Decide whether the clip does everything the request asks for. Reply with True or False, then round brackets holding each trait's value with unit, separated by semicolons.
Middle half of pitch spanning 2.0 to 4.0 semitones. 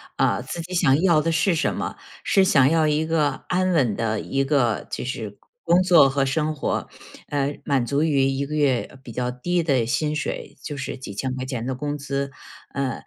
True (3.3 semitones)